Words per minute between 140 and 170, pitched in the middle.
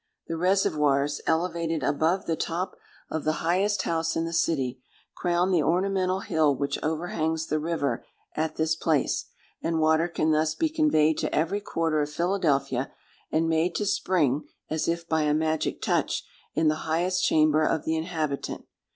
Yes: average, 165 wpm; medium, 160 Hz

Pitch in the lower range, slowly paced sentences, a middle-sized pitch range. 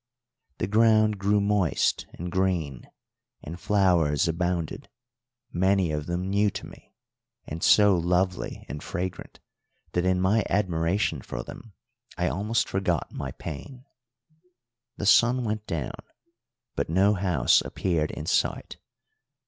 Yes: very low, 95 Hz; slow, 125 wpm; average, 3.5 semitones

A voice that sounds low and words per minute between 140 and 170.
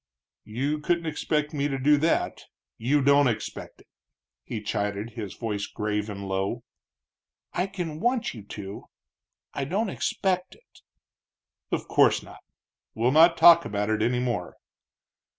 Yes: low, 130 Hz; average, 150 wpm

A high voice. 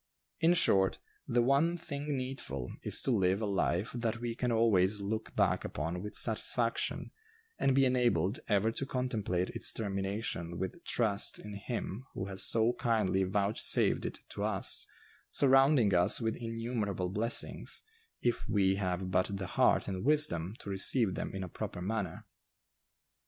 No: low, 105 Hz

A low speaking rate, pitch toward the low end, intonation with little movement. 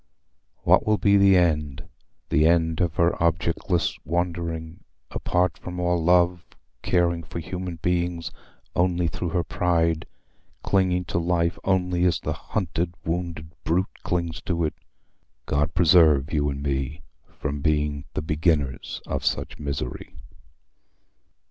Yes: slow, 130 wpm; very low, 85 Hz; narrow, 2.2 semitones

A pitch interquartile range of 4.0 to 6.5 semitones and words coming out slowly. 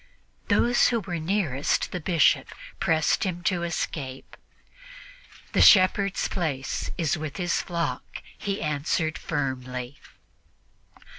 Yes: average, 4.5 semitones; slow, 105 wpm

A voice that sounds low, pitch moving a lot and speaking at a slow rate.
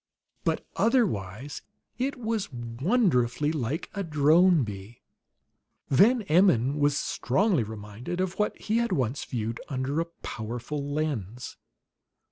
No: medium, 145 Hz; wide, 7.9 semitones; slow, 115 wpm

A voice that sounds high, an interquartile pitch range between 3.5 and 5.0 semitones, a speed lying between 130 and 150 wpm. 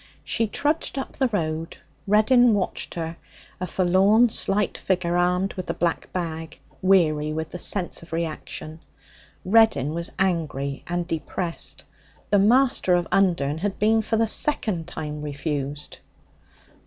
No: medium, 175 Hz; average, 4.3 semitones; average, 140 wpm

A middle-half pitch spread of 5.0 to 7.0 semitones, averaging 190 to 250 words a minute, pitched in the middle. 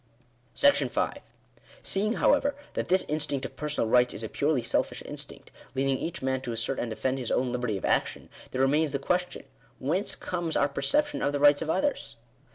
Yes: average, 5.3 semitones; average, 195 wpm; medium, 145 Hz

